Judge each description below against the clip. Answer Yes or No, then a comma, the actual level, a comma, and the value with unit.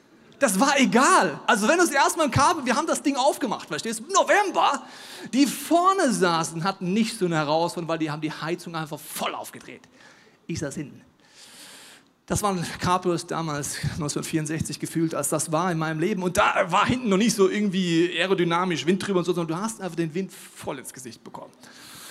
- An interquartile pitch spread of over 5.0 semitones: Yes, wide, 5.6 semitones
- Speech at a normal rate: No, fast, 195 wpm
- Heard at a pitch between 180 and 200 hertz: Yes, medium, 185 Hz